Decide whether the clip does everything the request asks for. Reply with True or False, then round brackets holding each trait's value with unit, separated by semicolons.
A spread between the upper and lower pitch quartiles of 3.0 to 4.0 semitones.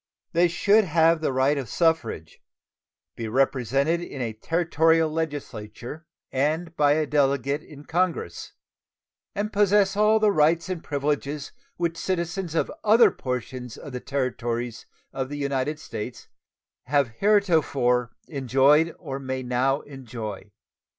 False (4.4 semitones)